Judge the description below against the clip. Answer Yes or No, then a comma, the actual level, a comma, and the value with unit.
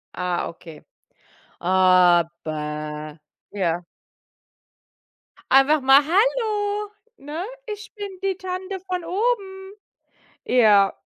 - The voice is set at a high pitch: Yes, very high, 285 Hz